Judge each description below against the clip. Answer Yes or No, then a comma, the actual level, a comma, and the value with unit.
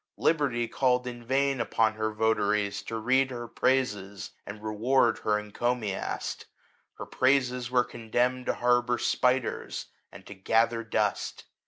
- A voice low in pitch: Yes, low, 120 Hz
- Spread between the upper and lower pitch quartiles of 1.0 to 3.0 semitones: Yes, narrow, 2.6 semitones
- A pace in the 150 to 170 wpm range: No, slow, 135 wpm